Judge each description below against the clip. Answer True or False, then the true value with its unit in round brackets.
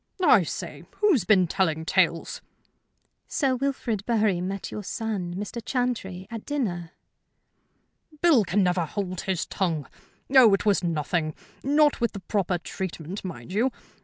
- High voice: True (195 Hz)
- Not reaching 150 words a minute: True (140 wpm)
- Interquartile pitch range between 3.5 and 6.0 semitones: True (4.9 semitones)